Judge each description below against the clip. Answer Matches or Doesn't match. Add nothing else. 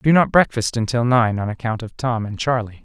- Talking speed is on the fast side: Matches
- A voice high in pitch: Doesn't match